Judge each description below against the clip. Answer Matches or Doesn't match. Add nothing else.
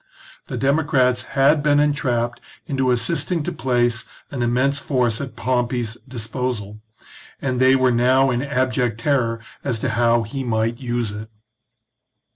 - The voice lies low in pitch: Matches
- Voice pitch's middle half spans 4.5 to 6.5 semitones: Doesn't match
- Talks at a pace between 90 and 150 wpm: Matches